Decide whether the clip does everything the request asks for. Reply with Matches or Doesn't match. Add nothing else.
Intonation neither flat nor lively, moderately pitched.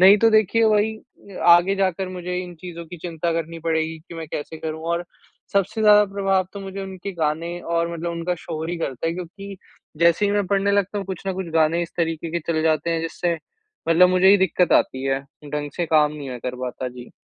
Matches